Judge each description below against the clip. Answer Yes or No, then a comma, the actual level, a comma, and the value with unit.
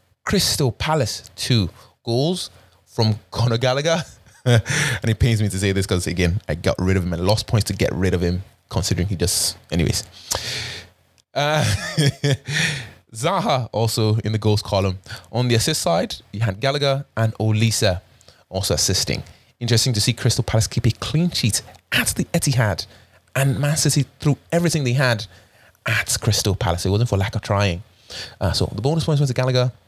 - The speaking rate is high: No, average, 175 wpm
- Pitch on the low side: Yes, low, 110 Hz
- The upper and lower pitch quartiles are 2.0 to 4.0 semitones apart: No, average, 4.8 semitones